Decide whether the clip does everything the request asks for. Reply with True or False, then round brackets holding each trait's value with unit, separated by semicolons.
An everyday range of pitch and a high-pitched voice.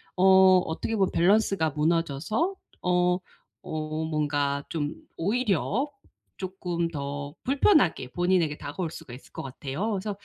False (4.3 semitones; 170 Hz)